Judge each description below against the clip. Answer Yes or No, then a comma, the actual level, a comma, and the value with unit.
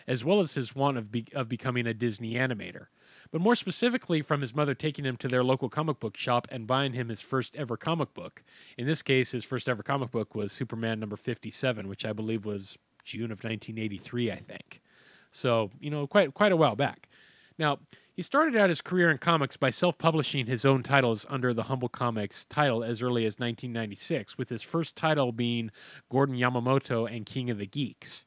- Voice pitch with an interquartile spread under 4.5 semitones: Yes, average, 3.9 semitones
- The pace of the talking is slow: No, fast, 205 wpm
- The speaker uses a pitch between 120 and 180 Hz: Yes, low, 130 Hz